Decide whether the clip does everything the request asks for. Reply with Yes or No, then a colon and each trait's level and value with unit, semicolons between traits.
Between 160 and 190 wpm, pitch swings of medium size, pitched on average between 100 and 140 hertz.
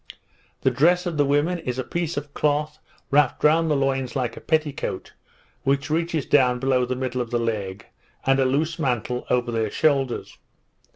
Yes: average, 180 wpm; average, 3.5 semitones; low, 135 Hz